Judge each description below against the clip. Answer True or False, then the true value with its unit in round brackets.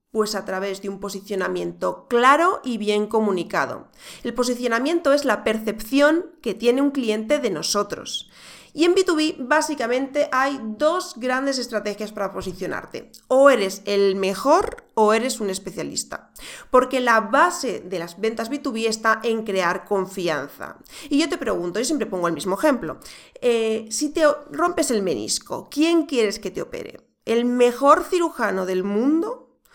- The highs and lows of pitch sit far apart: True (6.3 semitones)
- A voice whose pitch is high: True (235 Hz)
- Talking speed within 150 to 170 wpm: True (155 wpm)